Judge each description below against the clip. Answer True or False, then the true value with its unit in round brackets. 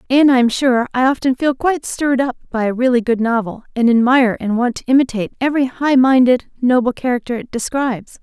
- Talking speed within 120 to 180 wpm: False (205 wpm)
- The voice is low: False (250 Hz)